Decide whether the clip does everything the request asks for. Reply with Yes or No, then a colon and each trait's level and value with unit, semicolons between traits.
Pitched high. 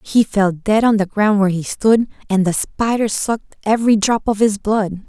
Yes: high, 210 Hz